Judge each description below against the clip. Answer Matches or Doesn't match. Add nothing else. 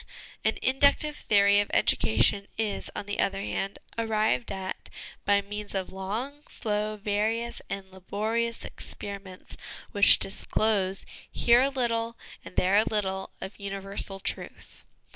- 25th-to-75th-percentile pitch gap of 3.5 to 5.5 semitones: Doesn't match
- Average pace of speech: Doesn't match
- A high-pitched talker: Matches